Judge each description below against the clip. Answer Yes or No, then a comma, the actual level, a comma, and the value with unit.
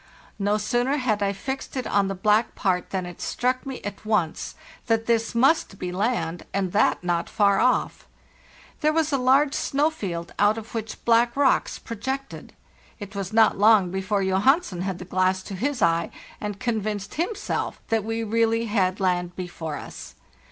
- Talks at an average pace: Yes, average, 175 wpm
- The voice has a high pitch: Yes, high, 210 Hz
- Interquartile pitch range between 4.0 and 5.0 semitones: Yes, average, 4.4 semitones